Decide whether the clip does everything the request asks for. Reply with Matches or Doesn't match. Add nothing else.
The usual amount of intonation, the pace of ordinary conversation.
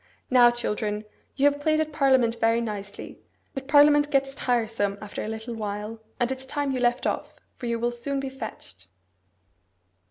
Matches